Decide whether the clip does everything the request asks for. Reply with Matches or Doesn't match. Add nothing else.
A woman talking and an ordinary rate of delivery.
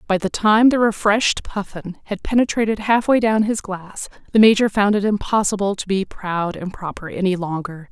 Matches